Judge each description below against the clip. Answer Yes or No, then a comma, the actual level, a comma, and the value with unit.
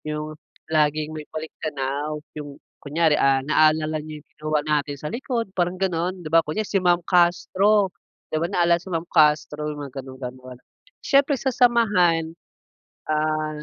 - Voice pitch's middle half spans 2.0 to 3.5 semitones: Yes, average, 2.9 semitones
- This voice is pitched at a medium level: Yes, medium, 155 Hz